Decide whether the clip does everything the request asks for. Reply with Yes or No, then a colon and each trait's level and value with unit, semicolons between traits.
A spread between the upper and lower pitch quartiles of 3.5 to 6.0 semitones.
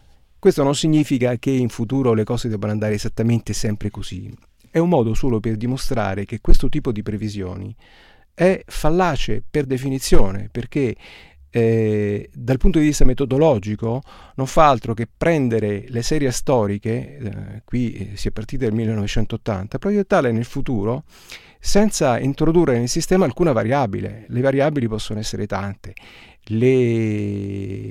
Yes: average, 4.4 semitones